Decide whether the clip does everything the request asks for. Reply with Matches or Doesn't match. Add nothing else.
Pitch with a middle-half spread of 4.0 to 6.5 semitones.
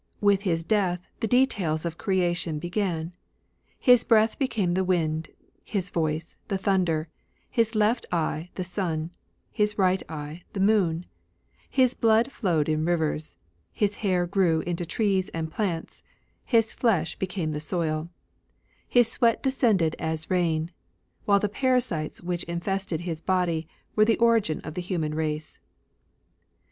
Matches